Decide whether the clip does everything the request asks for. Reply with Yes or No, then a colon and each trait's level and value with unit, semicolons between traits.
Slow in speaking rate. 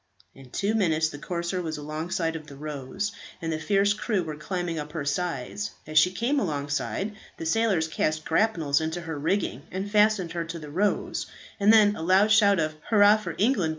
No: average, 190 wpm